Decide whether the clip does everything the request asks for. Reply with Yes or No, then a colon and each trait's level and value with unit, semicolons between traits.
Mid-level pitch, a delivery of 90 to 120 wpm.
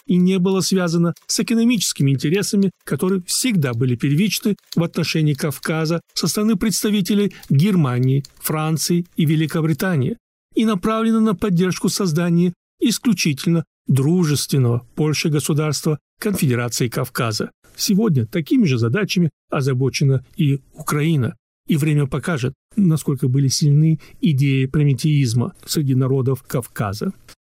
Yes: medium, 160 Hz; slow, 110 wpm